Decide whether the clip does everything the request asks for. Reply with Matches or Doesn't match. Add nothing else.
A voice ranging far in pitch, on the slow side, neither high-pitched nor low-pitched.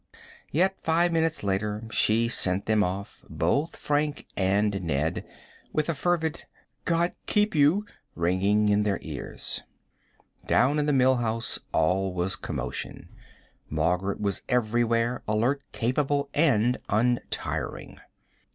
Doesn't match